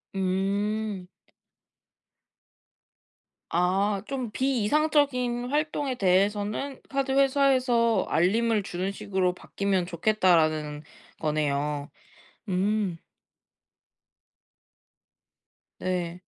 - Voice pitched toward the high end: Yes, high, 200 Hz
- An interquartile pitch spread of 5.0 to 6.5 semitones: Yes, wide, 5.5 semitones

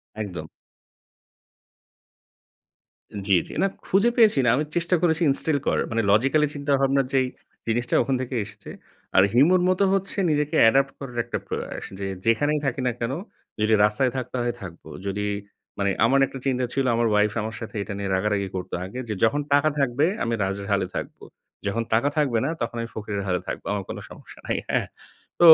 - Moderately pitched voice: No, low, 120 Hz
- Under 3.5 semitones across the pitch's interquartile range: No, average, 5.2 semitones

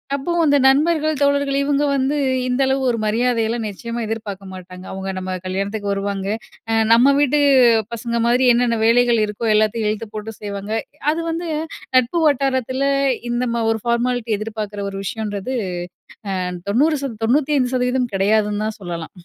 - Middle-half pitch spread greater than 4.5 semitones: No, average, 4.2 semitones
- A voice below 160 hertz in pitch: No, high, 235 Hz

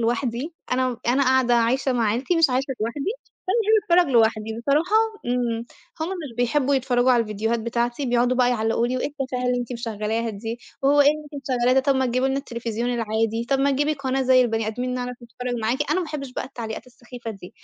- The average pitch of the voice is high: Yes, very high, 250 Hz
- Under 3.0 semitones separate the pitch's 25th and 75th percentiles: Yes, narrow, 2.6 semitones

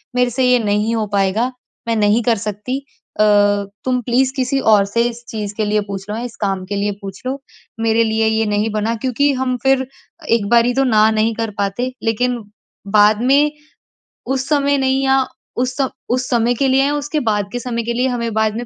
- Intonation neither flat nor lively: Yes, average, 3.4 semitones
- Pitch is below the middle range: No, high, 230 Hz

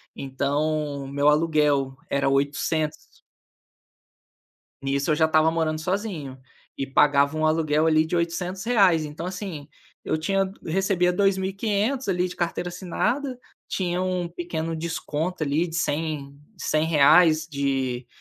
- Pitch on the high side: No, medium, 160 Hz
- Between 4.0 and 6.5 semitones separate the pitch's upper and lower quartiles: No, average, 3.6 semitones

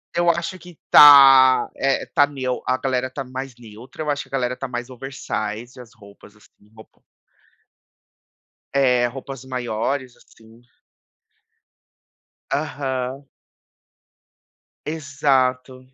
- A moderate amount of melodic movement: No, narrow, 2.0 semitones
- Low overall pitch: Yes, low, 130 Hz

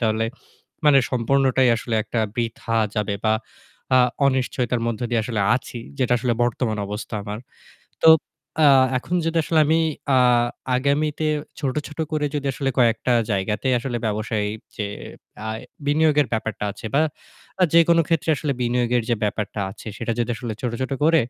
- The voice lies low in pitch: Yes, low, 125 Hz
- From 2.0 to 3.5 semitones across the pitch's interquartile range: No, average, 4.2 semitones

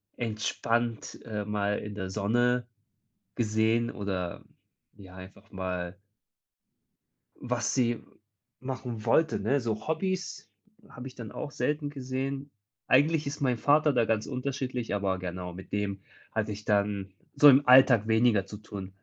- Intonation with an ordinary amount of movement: Yes, average, 4.4 semitones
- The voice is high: No, low, 115 Hz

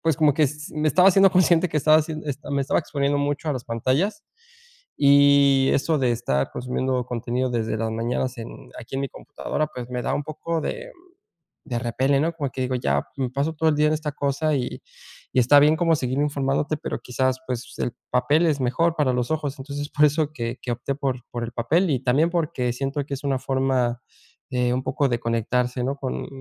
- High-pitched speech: No, medium, 140 Hz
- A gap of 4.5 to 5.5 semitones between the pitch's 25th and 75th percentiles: No, average, 3.4 semitones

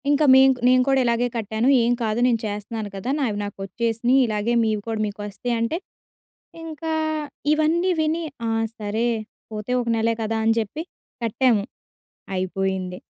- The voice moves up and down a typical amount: Yes, average, 3.5 semitones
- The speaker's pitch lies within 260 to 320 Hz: No, high, 230 Hz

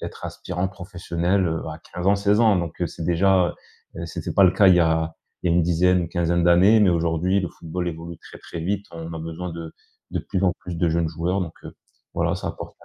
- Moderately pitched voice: No, very low, 85 Hz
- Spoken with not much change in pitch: Yes, narrow, 1.8 semitones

